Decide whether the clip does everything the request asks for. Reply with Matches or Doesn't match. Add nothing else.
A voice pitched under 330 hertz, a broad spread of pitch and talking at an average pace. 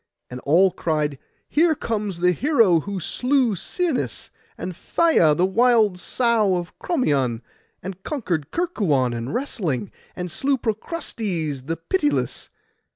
Doesn't match